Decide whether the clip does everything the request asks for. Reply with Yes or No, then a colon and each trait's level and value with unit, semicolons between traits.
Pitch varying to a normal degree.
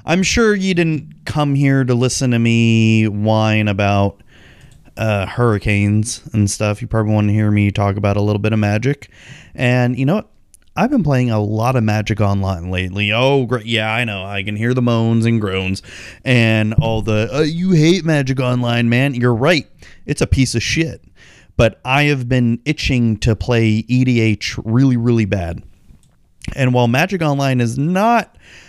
Yes: average, 3.8 semitones